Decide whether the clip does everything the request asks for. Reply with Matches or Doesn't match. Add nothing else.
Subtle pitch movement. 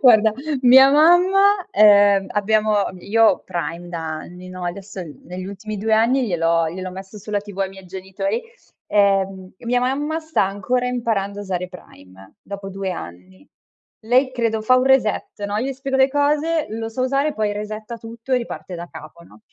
Doesn't match